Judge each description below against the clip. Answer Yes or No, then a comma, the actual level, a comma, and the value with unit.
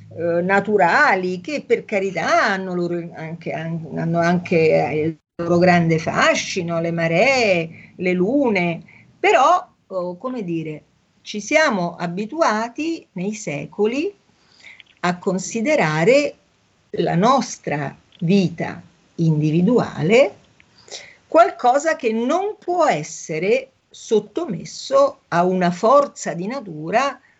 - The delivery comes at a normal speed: No, slow, 95 wpm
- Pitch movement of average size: No, wide, 7.0 semitones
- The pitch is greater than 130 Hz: Yes, high, 190 Hz